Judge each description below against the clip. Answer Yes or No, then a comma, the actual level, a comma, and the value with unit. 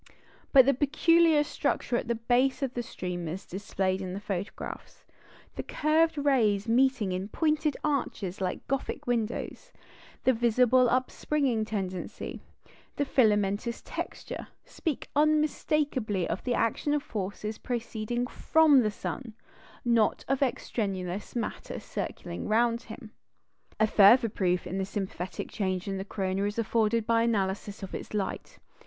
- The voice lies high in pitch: Yes, high, 230 Hz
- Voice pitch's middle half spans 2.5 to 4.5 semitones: No, average, 4.9 semitones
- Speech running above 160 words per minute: No, slow, 135 wpm